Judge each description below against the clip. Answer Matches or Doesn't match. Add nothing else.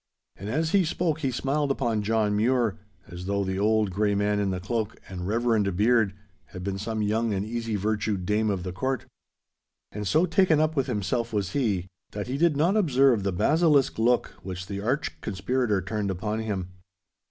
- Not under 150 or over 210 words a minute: Matches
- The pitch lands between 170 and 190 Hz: Doesn't match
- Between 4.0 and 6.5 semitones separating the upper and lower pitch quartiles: Matches